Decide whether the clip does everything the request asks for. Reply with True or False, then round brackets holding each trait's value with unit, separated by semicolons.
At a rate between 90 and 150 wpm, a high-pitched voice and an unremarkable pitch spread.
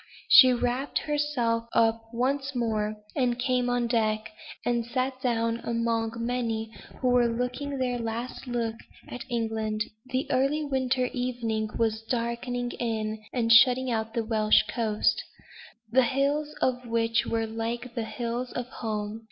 False (145 wpm; 235 Hz; 2.0 semitones)